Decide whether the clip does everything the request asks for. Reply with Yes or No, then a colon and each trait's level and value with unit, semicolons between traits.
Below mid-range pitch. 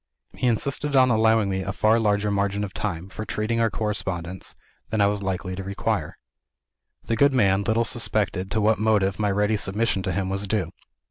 Yes: low, 105 Hz